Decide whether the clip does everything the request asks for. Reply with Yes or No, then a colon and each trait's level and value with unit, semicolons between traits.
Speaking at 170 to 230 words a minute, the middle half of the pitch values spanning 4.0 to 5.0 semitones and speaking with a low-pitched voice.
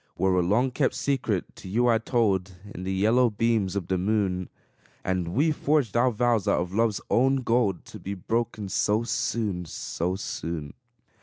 Yes: average, 175 wpm; average, 4.3 semitones; low, 105 Hz